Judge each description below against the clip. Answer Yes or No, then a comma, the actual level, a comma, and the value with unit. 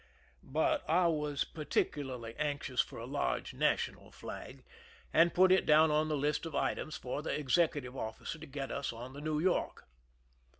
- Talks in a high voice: No, medium, 150 Hz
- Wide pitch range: No, average, 2.7 semitones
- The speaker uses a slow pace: No, average, 170 wpm